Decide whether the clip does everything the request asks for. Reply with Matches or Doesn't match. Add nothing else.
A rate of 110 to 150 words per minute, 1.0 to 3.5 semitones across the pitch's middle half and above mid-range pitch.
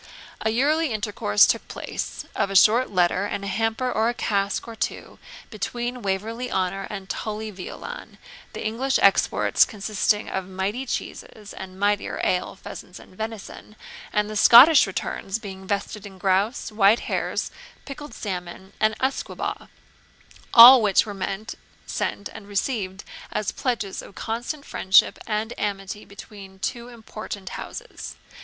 Matches